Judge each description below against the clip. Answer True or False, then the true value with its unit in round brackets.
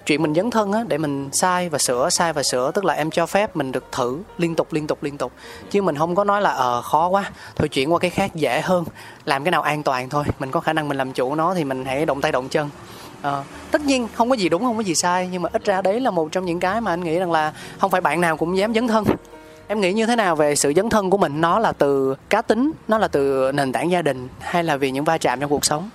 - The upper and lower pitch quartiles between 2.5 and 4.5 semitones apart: False (5.3 semitones)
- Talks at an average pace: False (305 wpm)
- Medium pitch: True (165 Hz)